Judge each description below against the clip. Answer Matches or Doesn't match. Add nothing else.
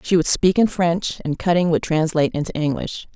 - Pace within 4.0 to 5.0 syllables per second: Doesn't match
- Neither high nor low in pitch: Matches